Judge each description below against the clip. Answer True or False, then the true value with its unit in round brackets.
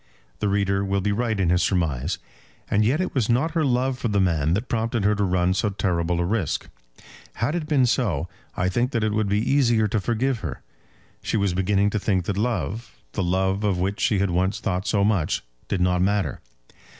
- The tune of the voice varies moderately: True (3.8 semitones)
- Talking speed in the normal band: False (215 wpm)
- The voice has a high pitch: False (100 Hz)